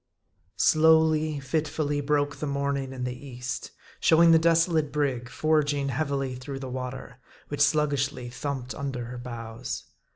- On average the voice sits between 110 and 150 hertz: Yes, medium, 140 Hz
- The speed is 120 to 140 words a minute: Yes, slow, 135 wpm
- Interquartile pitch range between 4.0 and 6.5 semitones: No, average, 3.0 semitones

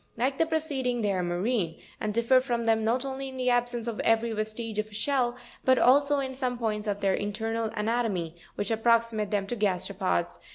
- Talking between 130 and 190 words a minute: No, average, 200 wpm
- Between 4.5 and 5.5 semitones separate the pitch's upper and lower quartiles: No, average, 3.2 semitones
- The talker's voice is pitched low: No, high, 225 Hz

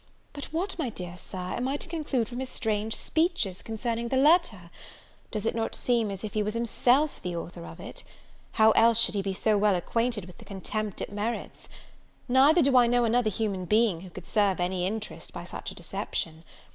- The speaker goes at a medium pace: No, fast, 210 wpm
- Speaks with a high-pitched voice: Yes, high, 220 Hz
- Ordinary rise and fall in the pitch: Yes, average, 4.2 semitones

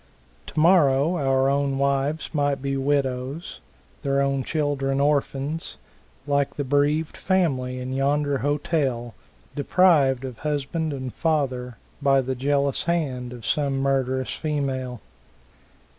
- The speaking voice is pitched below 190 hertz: Yes, medium, 140 Hz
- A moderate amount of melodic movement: No, narrow, 1.8 semitones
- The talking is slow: Yes, slow, 115 wpm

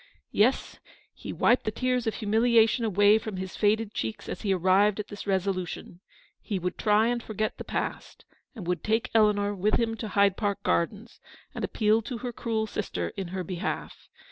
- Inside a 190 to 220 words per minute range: Yes, average, 195 wpm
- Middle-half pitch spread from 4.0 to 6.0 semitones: No, average, 2.7 semitones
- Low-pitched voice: No, high, 210 Hz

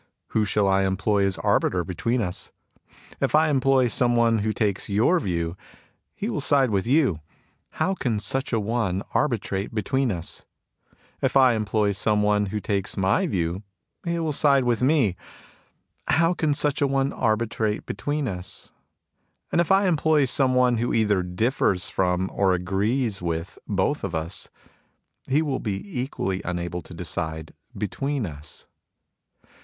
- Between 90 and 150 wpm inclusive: No, average, 160 wpm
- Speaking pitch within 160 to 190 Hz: No, low, 110 Hz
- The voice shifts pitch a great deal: Yes, wide, 5.9 semitones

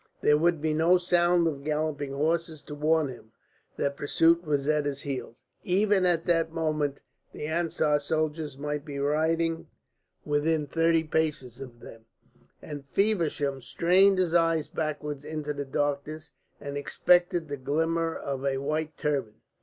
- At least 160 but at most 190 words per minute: No, average, 150 wpm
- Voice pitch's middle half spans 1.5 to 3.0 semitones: Yes, narrow, 2.5 semitones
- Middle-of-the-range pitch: Yes, medium, 155 Hz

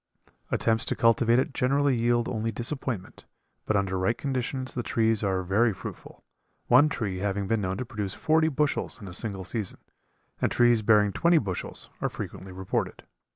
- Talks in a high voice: No, low, 115 Hz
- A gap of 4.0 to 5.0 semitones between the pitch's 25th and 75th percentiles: Yes, average, 4.3 semitones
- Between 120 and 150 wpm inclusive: No, average, 170 wpm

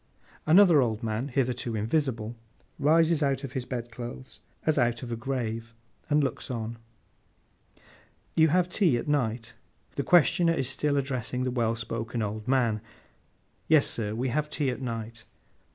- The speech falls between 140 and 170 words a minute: Yes, average, 155 wpm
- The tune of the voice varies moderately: Yes, average, 4.0 semitones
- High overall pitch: No, low, 125 Hz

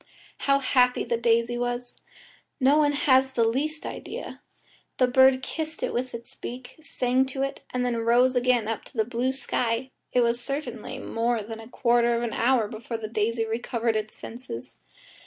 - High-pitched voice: Yes, high, 245 Hz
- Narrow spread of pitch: Yes, narrow, 2.3 semitones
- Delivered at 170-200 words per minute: Yes, average, 180 wpm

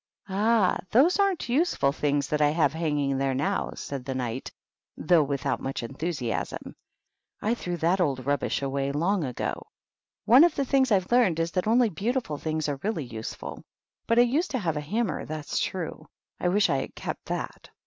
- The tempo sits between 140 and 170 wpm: No, average, 185 wpm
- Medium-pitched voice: Yes, medium, 165 Hz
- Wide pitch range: Yes, wide, 8.0 semitones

